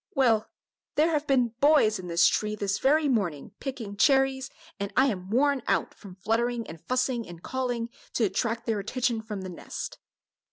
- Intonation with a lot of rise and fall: No, average, 4.7 semitones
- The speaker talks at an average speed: Yes, average, 175 wpm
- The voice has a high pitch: Yes, high, 230 Hz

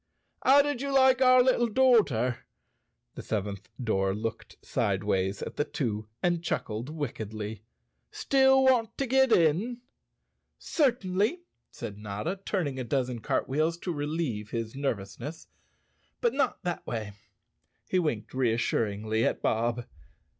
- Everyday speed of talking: No, slow, 130 wpm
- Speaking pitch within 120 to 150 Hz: Yes, medium, 140 Hz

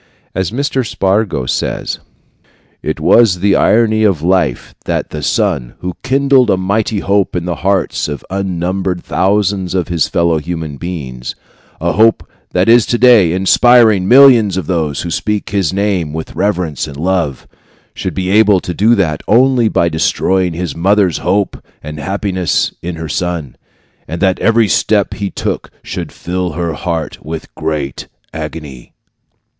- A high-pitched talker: No, very low, 95 Hz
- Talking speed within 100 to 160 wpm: Yes, average, 155 wpm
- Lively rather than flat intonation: No, average, 4.0 semitones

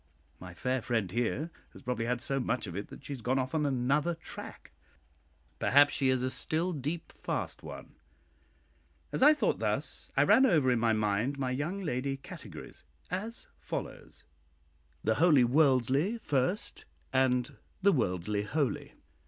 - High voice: No, low, 130 Hz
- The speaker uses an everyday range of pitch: Yes, average, 4.0 semitones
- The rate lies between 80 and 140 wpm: No, average, 160 wpm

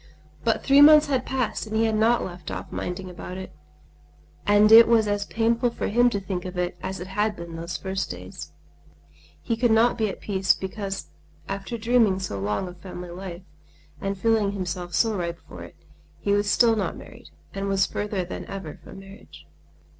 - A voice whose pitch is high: Yes, high, 200 Hz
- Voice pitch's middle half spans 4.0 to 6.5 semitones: No, average, 3.3 semitones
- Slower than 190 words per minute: No, average, 195 wpm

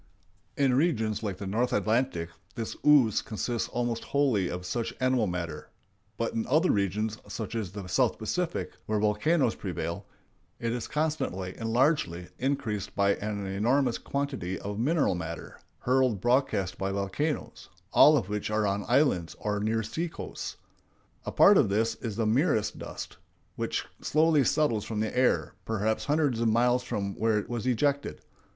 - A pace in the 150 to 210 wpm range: Yes, average, 160 wpm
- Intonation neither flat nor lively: Yes, average, 4.4 semitones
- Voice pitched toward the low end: Yes, low, 115 Hz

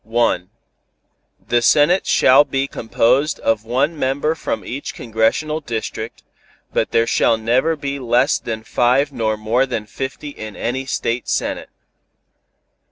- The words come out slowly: Yes, slow, 130 wpm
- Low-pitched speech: Yes, low, 125 Hz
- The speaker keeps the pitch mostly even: No, average, 3.7 semitones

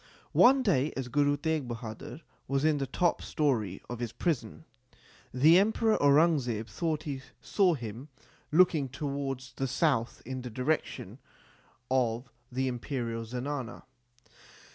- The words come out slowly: Yes, slow, 130 wpm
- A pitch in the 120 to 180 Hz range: Yes, low, 135 Hz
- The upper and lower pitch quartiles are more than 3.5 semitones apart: Yes, average, 4.1 semitones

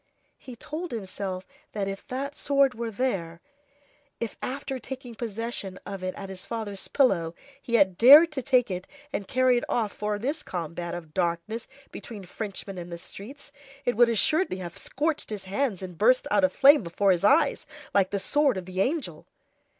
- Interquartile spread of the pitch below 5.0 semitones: No, wide, 5.6 semitones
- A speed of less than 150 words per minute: No, average, 180 wpm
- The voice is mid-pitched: No, high, 215 Hz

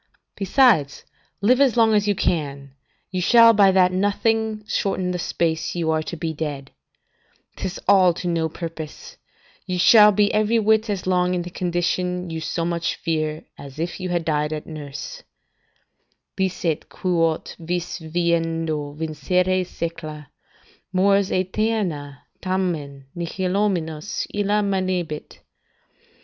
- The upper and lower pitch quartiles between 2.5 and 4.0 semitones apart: Yes, average, 3.6 semitones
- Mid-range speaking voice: Yes, medium, 180 Hz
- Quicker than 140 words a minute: No, slow, 135 wpm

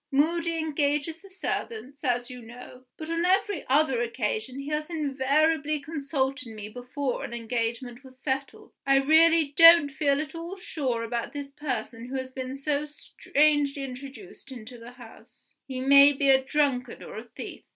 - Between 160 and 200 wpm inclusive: Yes, average, 165 wpm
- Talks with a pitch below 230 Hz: No, very high, 275 Hz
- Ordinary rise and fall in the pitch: Yes, average, 3.3 semitones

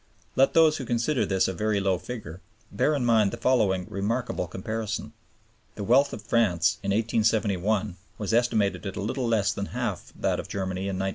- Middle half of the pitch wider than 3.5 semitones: No, average, 3.2 semitones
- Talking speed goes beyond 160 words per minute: Yes, average, 190 wpm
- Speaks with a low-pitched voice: Yes, low, 105 Hz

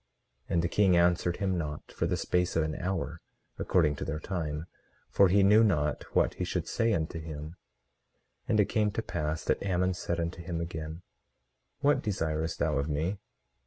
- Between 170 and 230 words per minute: Yes, average, 190 wpm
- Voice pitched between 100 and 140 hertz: No, very low, 85 Hz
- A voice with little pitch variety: No, average, 3.2 semitones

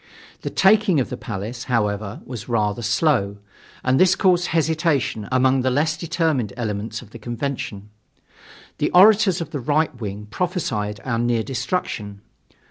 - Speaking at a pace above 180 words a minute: No, average, 145 wpm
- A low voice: Yes, low, 125 Hz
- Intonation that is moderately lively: No, wide, 6.9 semitones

